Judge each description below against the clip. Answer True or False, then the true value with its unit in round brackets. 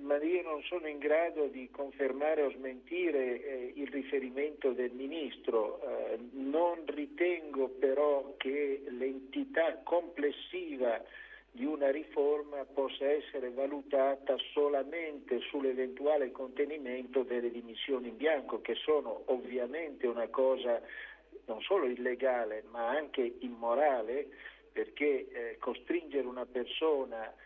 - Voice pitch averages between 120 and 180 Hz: True (140 Hz)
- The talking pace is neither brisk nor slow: False (110 wpm)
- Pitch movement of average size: True (4.4 semitones)